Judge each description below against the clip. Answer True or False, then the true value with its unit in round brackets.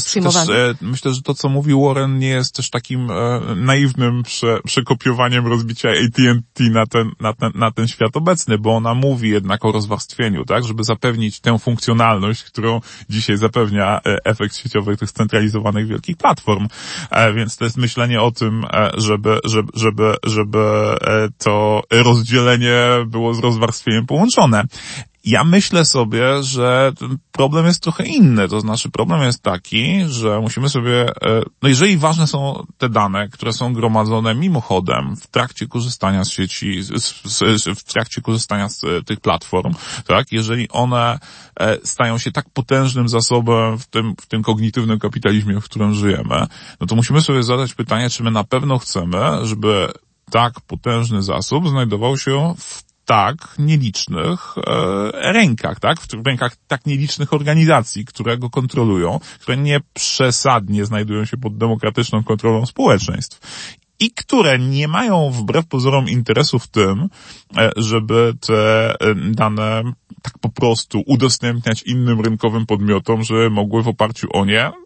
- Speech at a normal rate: True (150 wpm)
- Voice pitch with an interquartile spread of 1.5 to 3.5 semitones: True (3.2 semitones)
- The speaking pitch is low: True (115 Hz)